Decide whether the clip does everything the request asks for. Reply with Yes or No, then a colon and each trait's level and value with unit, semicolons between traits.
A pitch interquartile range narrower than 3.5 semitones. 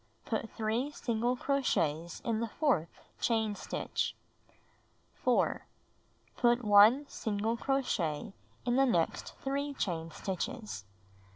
No: average, 4.7 semitones